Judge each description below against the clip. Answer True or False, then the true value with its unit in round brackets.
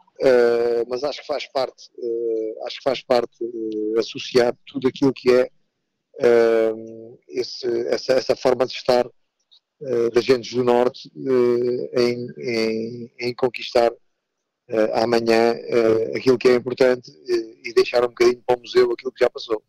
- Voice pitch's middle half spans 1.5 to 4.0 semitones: True (2.8 semitones)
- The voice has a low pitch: True (125 Hz)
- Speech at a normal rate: True (160 wpm)